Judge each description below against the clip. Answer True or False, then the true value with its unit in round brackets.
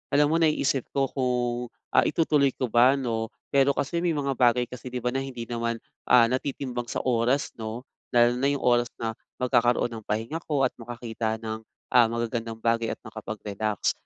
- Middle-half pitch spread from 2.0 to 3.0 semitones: True (2.7 semitones)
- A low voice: True (120 Hz)